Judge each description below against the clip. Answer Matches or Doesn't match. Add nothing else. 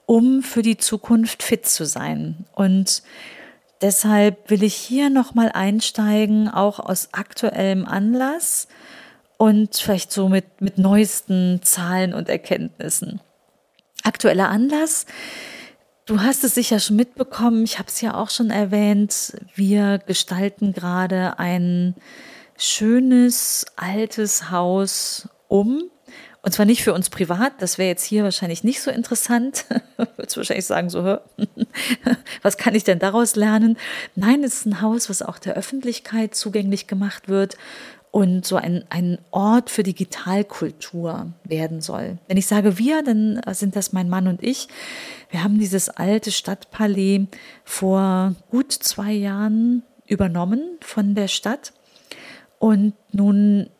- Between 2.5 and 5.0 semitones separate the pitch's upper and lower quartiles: Matches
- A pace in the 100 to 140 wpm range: Matches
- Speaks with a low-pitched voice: Doesn't match